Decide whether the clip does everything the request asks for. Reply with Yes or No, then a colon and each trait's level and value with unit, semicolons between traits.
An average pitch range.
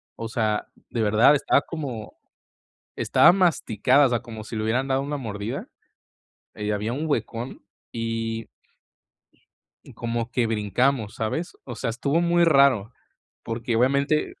Yes: average, 3.8 semitones